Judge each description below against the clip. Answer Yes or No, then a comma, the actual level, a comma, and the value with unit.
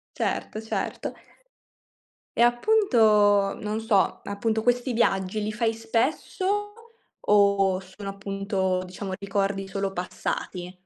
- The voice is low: No, high, 205 Hz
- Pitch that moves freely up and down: No, narrow, 2.6 semitones